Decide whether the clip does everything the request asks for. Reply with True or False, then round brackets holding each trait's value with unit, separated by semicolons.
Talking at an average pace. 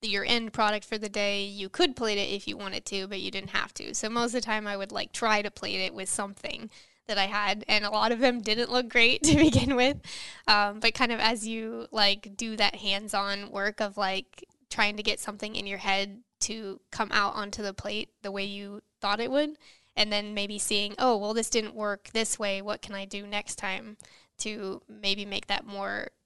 False (235 wpm)